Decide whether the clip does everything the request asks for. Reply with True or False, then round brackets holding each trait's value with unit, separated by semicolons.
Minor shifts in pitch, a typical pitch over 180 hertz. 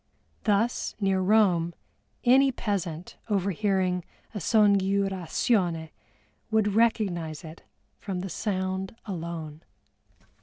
False (3.3 semitones; 190 Hz)